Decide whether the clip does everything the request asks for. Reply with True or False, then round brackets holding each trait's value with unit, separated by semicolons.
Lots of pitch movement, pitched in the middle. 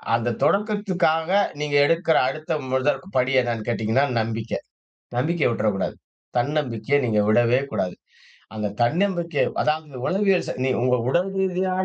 True (6.6 semitones; 145 Hz)